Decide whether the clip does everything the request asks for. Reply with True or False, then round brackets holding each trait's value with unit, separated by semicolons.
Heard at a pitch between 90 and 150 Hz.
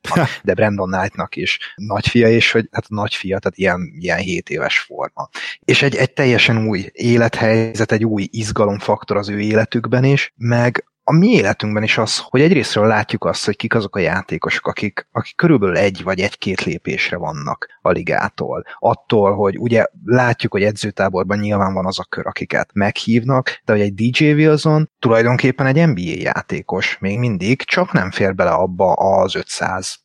True (115 Hz)